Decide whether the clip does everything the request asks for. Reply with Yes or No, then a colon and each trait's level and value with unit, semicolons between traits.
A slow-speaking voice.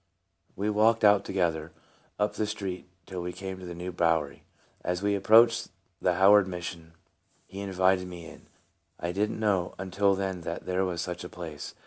No: average, 180 wpm